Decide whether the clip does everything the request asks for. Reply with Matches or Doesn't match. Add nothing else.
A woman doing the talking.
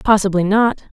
Matches